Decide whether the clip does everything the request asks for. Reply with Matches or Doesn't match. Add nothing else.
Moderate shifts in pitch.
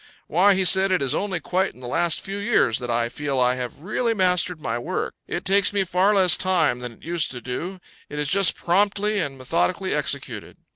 Doesn't match